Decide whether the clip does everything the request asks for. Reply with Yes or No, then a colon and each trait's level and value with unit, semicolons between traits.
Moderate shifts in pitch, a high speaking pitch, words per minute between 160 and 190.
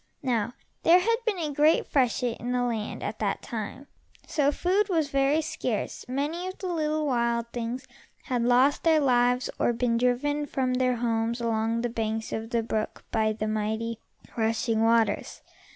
Yes: average, 4.2 semitones; high, 245 Hz; average, 175 wpm